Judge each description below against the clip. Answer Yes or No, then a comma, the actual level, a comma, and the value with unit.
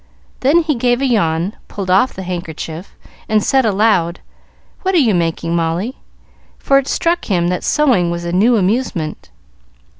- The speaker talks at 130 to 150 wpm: No, average, 160 wpm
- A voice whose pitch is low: No, high, 195 Hz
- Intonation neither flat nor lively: No, wide, 6.7 semitones